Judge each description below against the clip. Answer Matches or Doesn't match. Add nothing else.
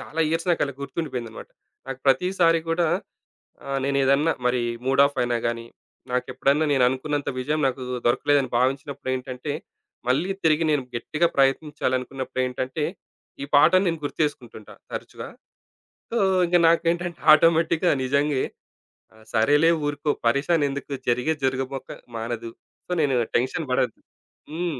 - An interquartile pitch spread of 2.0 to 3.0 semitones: Doesn't match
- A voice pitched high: Doesn't match